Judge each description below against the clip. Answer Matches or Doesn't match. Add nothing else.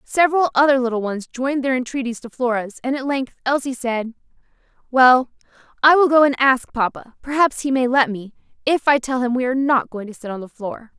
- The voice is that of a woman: Matches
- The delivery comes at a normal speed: Doesn't match